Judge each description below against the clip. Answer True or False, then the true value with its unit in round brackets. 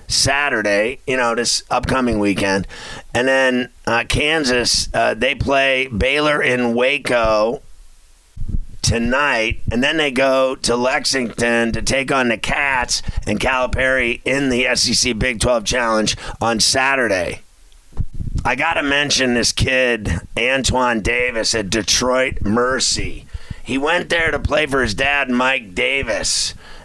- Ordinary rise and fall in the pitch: True (3.5 semitones)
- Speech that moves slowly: True (130 wpm)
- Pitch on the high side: False (120 Hz)